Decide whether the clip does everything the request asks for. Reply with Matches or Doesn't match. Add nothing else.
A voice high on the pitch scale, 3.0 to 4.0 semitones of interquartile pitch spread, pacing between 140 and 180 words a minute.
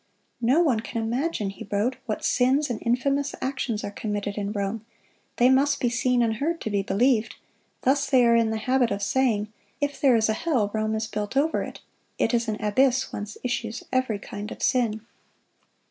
Doesn't match